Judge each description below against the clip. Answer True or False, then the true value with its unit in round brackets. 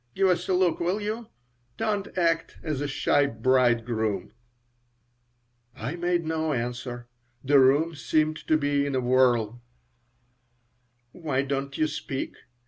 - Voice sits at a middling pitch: True (145 Hz)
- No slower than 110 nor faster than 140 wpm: True (135 wpm)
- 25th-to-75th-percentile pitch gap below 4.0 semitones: False (4.6 semitones)